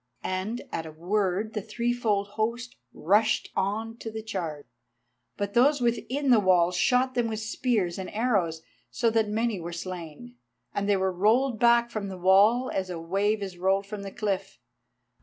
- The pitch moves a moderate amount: Yes, average, 3.7 semitones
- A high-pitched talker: Yes, high, 205 Hz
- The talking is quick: No, average, 175 wpm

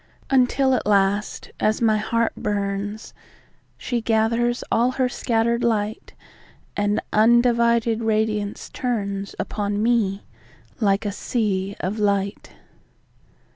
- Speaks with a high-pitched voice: Yes, high, 220 Hz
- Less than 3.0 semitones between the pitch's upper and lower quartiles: Yes, narrow, 2.4 semitones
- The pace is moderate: No, slow, 95 wpm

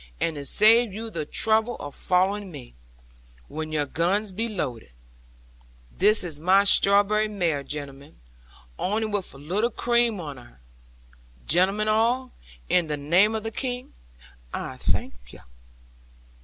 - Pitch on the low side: No, high, 195 Hz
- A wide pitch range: Yes, wide, 5.9 semitones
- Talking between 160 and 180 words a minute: No, average, 140 wpm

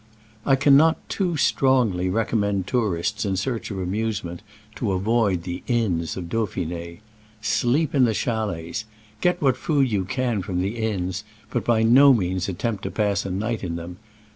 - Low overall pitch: Yes, low, 105 Hz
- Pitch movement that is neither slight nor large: Yes, average, 4.6 semitones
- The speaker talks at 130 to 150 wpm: No, average, 165 wpm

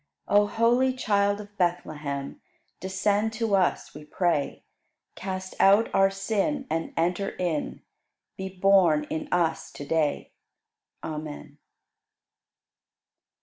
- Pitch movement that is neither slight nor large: Yes, average, 4.0 semitones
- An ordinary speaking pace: No, slow, 110 wpm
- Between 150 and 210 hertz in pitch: Yes, high, 190 Hz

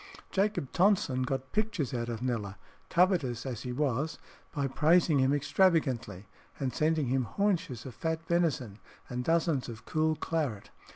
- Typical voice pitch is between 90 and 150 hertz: Yes, medium, 140 Hz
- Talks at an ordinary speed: Yes, average, 150 wpm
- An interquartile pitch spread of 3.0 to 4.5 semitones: No, average, 5.0 semitones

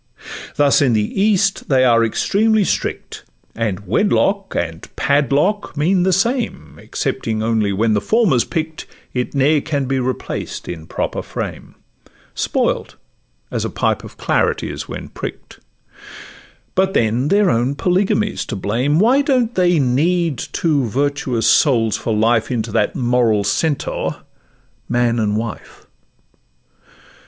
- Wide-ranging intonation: Yes, wide, 7.9 semitones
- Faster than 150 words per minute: No, average, 140 wpm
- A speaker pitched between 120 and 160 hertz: Yes, low, 135 Hz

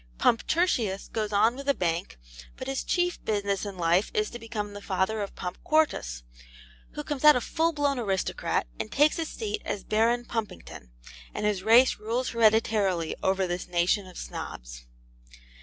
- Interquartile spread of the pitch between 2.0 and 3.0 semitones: No, wide, 5.5 semitones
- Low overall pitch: No, high, 215 Hz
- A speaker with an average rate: Yes, average, 175 wpm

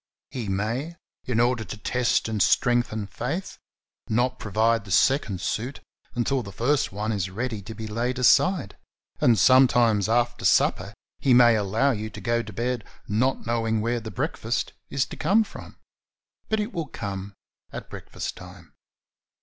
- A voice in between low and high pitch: No, low, 120 Hz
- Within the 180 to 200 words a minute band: No, average, 165 wpm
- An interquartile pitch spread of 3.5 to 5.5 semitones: No, average, 3.0 semitones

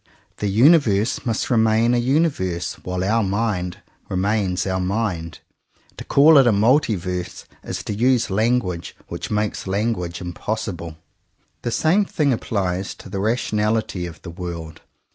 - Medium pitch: No, low, 105 Hz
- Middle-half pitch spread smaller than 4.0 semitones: No, average, 4.4 semitones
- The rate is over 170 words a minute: No, average, 140 wpm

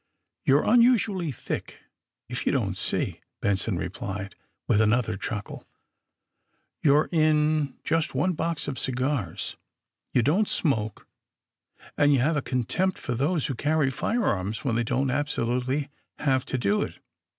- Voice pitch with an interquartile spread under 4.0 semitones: No, average, 5.1 semitones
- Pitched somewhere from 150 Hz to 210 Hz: No, low, 135 Hz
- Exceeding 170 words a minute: No, average, 145 wpm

